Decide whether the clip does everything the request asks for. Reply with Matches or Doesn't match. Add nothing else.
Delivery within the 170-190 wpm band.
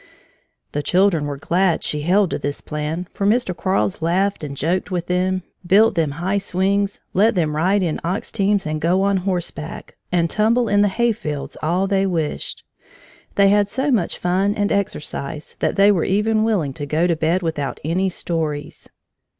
Matches